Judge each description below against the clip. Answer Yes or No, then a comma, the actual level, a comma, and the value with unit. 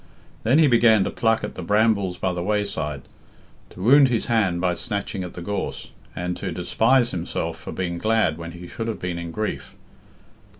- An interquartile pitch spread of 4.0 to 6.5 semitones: Yes, average, 4.3 semitones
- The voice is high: No, low, 100 Hz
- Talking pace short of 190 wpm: No, average, 195 wpm